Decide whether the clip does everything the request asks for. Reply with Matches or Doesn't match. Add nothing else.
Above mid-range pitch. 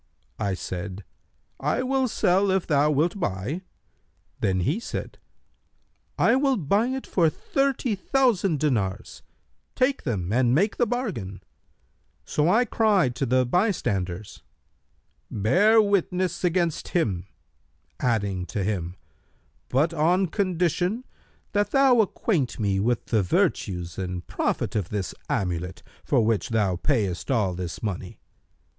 Doesn't match